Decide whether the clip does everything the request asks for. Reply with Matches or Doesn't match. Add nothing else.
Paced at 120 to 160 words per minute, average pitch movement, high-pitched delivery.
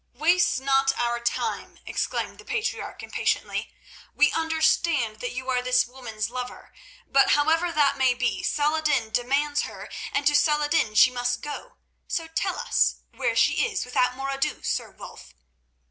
Matches